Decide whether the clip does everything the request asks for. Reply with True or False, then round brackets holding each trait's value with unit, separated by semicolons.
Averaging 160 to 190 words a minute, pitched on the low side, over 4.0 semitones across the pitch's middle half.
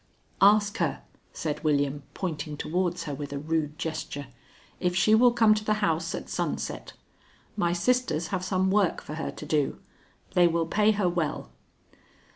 False (165 wpm; 175 Hz; 5.0 semitones)